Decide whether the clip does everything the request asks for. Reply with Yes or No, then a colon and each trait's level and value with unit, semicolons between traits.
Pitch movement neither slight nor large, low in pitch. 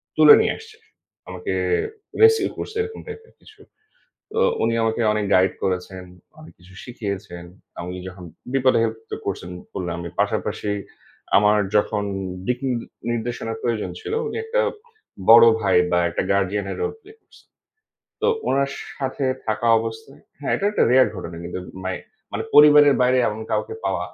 No: wide, 6.7 semitones; low, 115 Hz